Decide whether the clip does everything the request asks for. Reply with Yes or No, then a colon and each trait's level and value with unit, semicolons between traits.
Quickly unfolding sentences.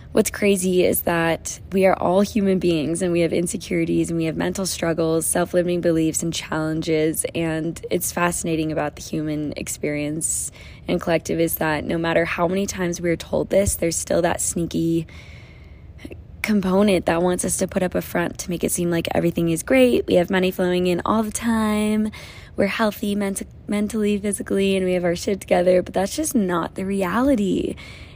No: average, 185 wpm